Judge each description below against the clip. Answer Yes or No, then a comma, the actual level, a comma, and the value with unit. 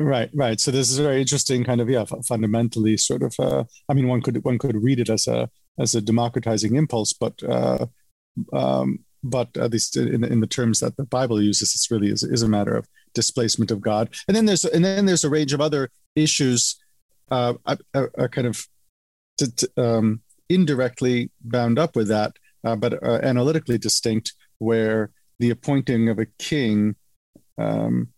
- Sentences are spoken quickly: No, average, 185 wpm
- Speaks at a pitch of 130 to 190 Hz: No, low, 120 Hz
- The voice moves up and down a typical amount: Yes, average, 3.5 semitones